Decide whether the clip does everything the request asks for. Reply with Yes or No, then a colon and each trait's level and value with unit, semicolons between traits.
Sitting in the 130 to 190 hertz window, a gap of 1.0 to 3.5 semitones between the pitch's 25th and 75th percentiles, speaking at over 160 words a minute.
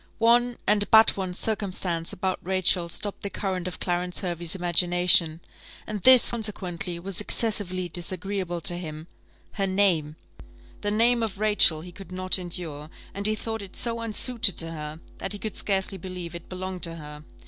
Yes: medium, 185 Hz; average, 3.0 semitones; average, 170 wpm